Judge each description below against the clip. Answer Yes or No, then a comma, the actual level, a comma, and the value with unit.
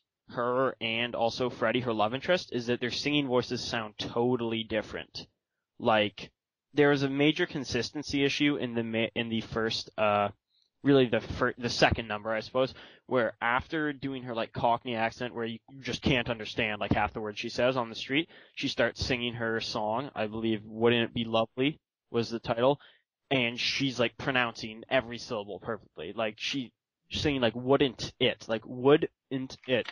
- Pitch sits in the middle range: No, low, 120 Hz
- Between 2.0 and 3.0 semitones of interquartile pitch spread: Yes, average, 2.7 semitones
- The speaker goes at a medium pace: Yes, average, 180 wpm